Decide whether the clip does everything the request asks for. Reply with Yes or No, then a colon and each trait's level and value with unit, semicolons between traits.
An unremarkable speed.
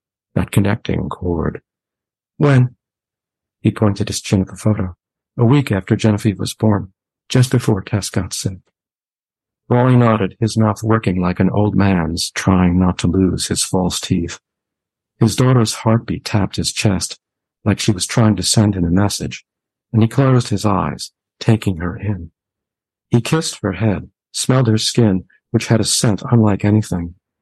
Yes: average, 160 wpm